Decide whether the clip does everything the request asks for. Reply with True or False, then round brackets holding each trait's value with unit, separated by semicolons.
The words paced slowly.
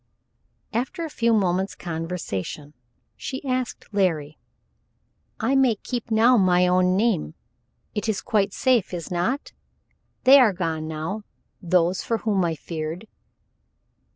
True (125 wpm)